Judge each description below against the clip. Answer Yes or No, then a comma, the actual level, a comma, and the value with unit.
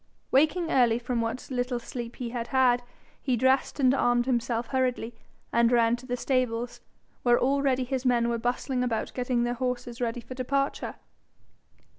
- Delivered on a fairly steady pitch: Yes, narrow, 1.5 semitones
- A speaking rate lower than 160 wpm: No, average, 165 wpm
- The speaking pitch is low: No, high, 245 Hz